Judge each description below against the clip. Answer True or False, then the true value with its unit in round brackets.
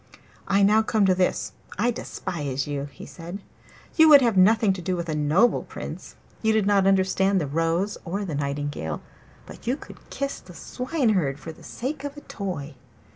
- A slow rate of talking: False (185 wpm)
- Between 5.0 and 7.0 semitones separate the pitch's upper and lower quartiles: True (5.6 semitones)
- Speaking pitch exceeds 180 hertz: True (190 Hz)